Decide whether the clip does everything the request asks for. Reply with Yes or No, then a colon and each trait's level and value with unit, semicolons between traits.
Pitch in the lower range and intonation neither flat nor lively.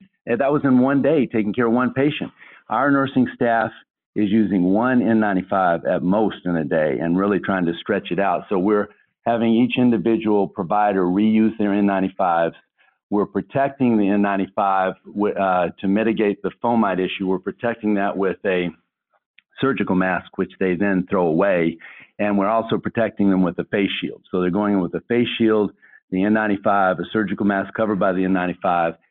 Yes: low, 105 Hz; average, 3.2 semitones